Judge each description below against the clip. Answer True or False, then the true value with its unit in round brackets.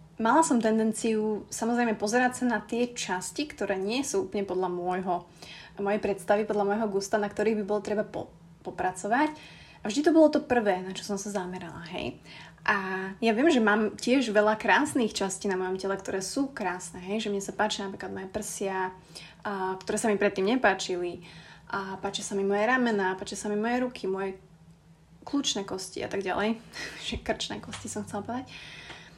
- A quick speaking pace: True (185 wpm)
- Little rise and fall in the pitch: False (3.0 semitones)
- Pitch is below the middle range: False (205 Hz)